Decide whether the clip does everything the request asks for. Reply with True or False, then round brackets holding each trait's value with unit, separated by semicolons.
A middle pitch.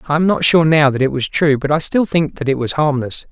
True (150 Hz)